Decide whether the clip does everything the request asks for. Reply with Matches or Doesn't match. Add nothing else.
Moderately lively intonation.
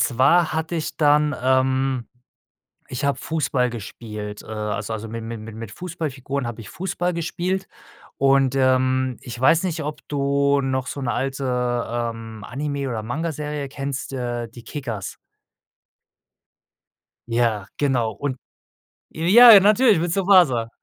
Matches